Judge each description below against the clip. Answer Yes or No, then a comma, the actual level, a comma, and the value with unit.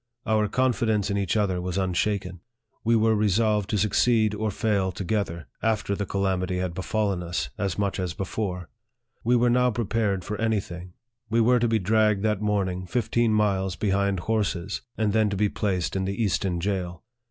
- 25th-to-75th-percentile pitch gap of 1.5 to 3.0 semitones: Yes, average, 2.7 semitones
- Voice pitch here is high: No, low, 100 Hz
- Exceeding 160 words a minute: Yes, average, 185 wpm